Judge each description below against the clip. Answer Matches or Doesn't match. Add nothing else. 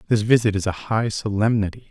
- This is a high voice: Doesn't match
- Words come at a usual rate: Matches